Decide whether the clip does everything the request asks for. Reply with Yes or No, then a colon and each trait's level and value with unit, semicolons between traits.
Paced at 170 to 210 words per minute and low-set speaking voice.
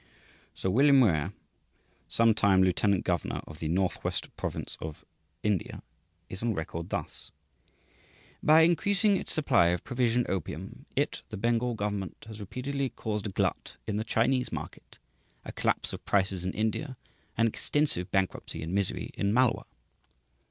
No: average, 145 wpm; low, 105 Hz